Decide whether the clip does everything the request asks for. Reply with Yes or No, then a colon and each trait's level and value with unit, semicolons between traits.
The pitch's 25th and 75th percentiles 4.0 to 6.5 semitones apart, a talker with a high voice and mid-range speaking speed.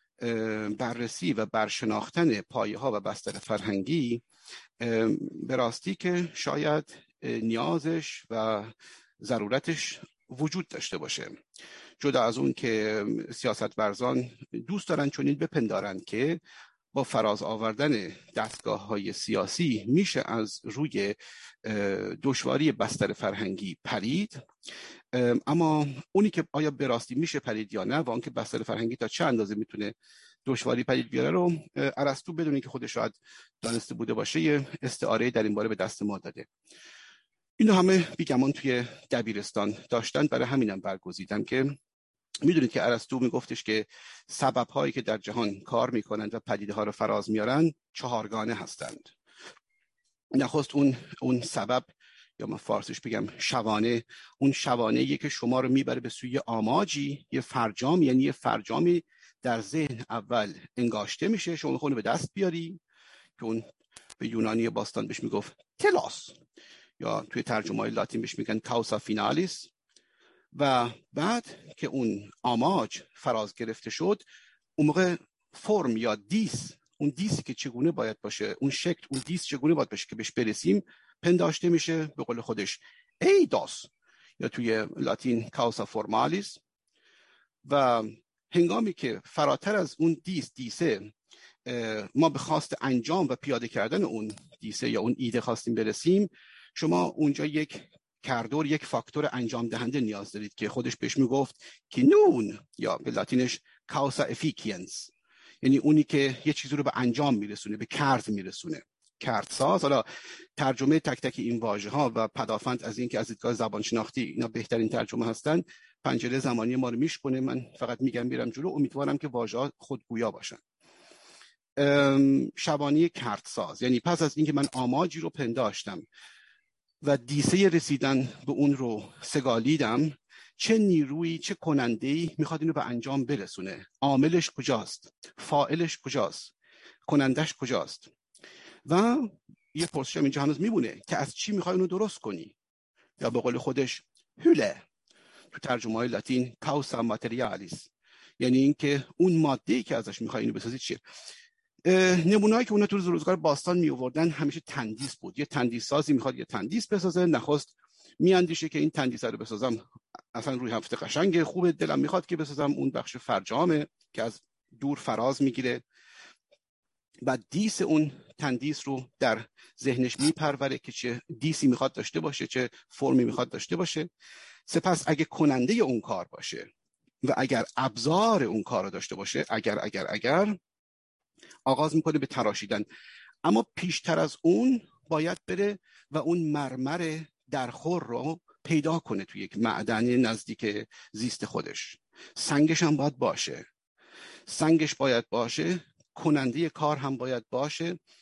No: wide, 5.5 semitones; medium, 140 Hz; average, 145 wpm